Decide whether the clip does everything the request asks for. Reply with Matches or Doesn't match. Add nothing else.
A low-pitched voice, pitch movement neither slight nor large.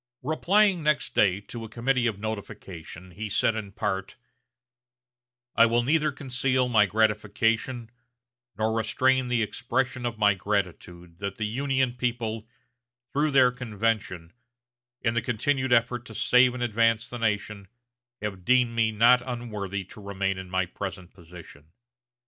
Matches